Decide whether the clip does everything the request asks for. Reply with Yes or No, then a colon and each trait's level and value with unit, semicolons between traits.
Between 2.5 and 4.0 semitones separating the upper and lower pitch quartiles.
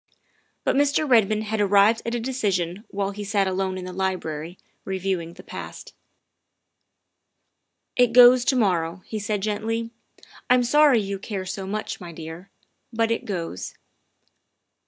Yes: average, 3.5 semitones